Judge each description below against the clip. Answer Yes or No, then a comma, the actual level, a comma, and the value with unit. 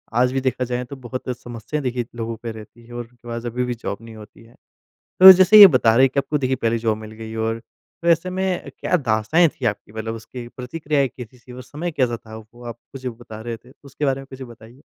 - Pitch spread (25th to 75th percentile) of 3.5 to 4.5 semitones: No, average, 3.0 semitones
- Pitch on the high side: No, low, 120 Hz